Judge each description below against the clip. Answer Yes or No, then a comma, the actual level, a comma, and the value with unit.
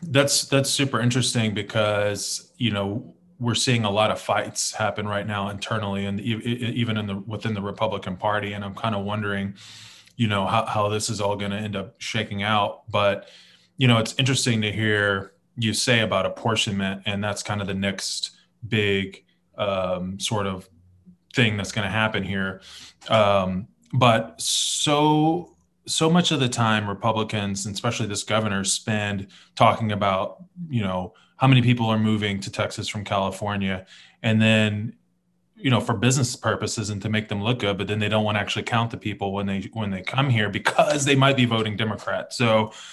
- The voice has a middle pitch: No, low, 110 Hz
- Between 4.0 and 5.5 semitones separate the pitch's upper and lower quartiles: No, narrow, 2.6 semitones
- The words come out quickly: No, average, 185 wpm